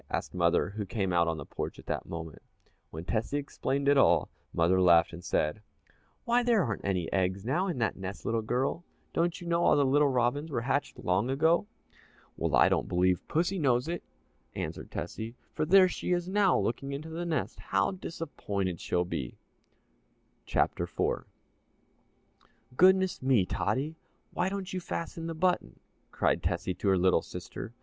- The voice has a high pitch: No, low, 130 Hz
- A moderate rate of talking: Yes, average, 175 wpm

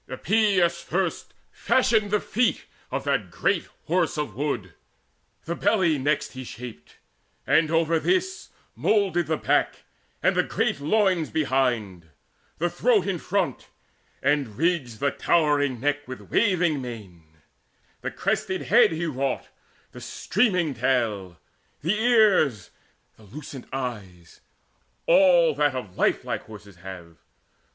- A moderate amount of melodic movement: No, wide, 6.8 semitones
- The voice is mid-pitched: Yes, medium, 150 Hz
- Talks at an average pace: No, slow, 125 wpm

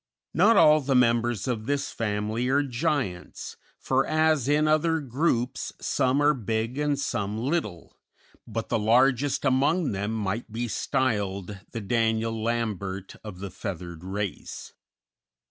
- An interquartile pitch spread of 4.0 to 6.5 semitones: Yes, average, 5.2 semitones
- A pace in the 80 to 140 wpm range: Yes, slow, 135 wpm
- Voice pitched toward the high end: No, low, 115 Hz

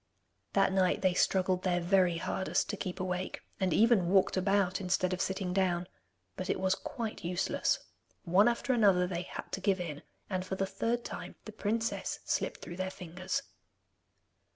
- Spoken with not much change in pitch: Yes, narrow, 1.7 semitones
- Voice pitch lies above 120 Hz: Yes, medium, 185 Hz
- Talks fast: No, average, 175 wpm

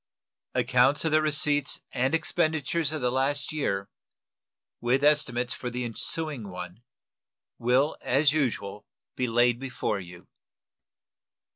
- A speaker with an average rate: No, slow, 120 wpm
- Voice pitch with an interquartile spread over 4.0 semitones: No, average, 3.7 semitones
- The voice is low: Yes, low, 130 Hz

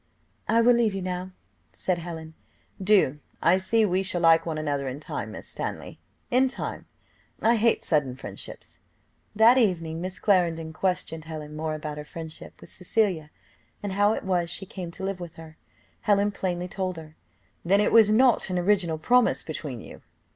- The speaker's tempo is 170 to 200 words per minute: Yes, average, 175 wpm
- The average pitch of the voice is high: No, medium, 180 Hz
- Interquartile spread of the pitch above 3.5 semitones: Yes, average, 4.2 semitones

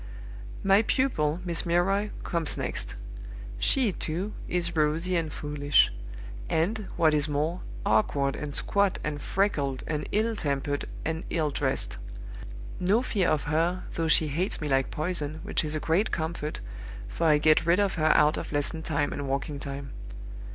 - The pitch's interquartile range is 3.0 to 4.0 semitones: Yes, average, 3.5 semitones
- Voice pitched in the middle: Yes, medium, 160 Hz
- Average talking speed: Yes, average, 160 wpm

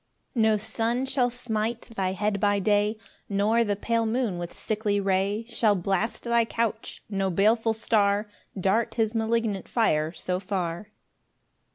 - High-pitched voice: Yes, high, 215 Hz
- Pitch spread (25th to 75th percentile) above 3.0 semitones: No, average, 2.7 semitones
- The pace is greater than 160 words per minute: No, average, 150 wpm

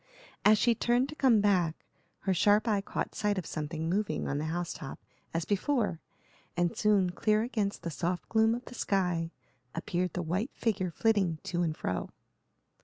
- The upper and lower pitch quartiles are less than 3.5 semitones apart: No, average, 4.2 semitones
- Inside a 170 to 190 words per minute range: Yes, average, 180 wpm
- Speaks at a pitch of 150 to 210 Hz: Yes, high, 190 Hz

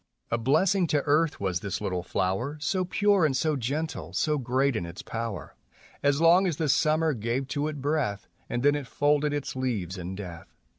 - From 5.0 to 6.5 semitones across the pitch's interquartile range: Yes, wide, 5.5 semitones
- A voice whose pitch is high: No, medium, 140 Hz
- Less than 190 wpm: No, average, 195 wpm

